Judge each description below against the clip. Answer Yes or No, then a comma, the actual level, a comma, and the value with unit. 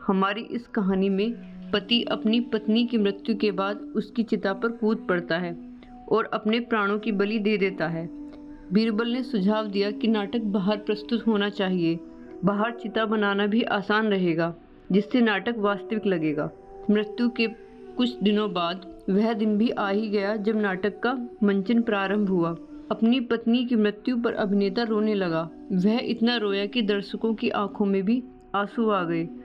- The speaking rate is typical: Yes, average, 165 wpm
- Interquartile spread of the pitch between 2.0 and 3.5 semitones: Yes, narrow, 2.5 semitones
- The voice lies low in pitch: No, high, 210 Hz